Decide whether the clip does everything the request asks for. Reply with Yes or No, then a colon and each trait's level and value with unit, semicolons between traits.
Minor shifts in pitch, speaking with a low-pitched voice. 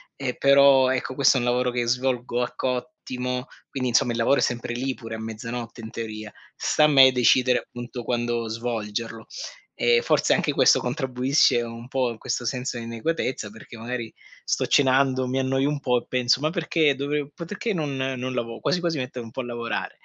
Yes: narrow, 2.2 semitones; low, 125 Hz